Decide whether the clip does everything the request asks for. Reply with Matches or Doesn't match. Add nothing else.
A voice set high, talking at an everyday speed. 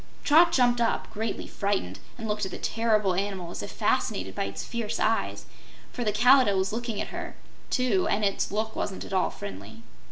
Matches